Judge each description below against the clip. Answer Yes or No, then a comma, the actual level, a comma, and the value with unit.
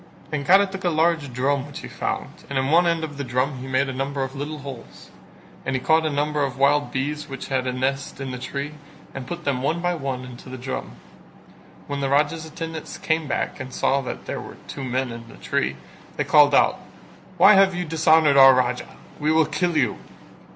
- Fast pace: Yes, fast, 225 wpm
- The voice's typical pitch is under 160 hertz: Yes, medium, 140 Hz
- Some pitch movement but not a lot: Yes, average, 3.2 semitones